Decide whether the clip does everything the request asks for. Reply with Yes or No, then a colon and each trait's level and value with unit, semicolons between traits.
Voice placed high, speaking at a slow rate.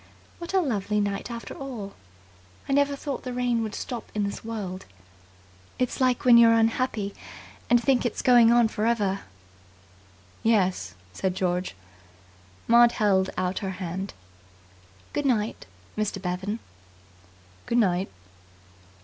Yes: high, 220 Hz; slow, 130 wpm